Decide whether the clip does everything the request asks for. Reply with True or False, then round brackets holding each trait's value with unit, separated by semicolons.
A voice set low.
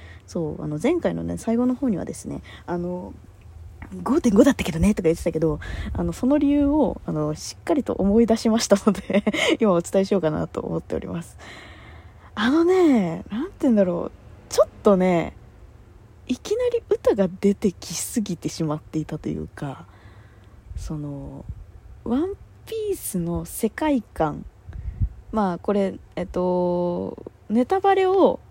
False (180 Hz)